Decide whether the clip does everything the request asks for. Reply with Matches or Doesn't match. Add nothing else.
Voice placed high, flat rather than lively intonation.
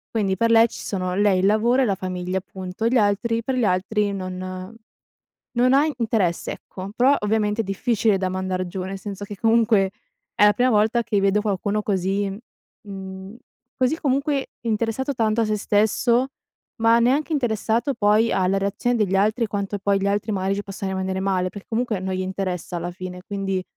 Doesn't match